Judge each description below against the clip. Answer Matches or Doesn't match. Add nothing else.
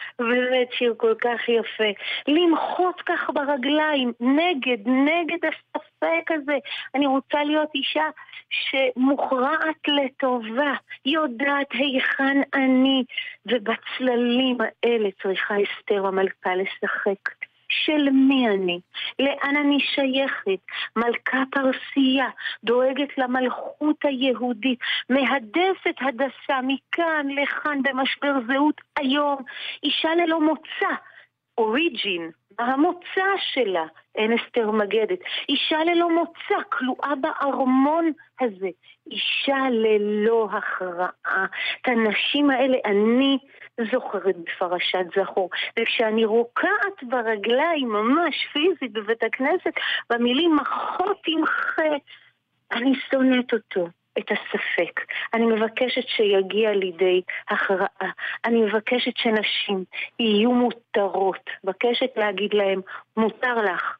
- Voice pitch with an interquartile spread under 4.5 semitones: Doesn't match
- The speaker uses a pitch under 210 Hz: Doesn't match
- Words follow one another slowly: Matches